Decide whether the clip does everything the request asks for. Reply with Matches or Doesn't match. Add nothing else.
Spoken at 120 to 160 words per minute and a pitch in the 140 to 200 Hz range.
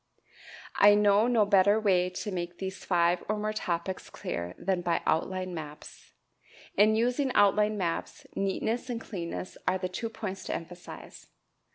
Matches